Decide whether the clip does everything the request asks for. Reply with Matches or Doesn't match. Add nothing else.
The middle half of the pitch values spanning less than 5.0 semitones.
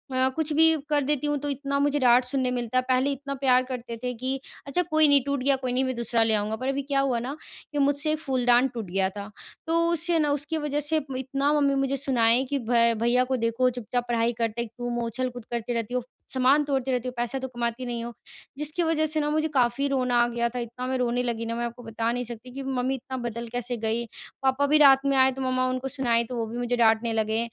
Matches